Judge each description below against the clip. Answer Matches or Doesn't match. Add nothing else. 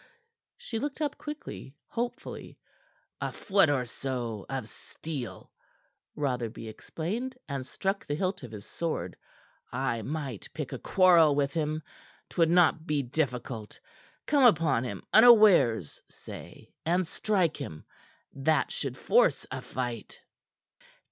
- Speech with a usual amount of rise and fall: Doesn't match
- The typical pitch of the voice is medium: Matches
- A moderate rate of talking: Doesn't match